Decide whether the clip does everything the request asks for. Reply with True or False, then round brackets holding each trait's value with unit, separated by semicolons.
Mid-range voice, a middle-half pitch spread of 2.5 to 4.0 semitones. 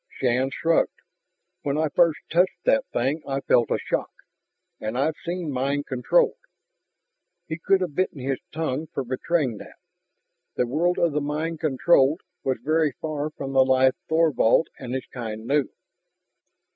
True (145 Hz; 3.7 semitones)